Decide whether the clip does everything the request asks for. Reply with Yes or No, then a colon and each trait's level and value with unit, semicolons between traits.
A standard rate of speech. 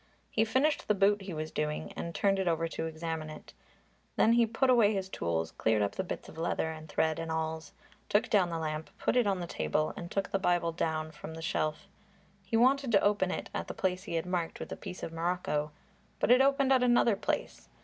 No: fast, 230 wpm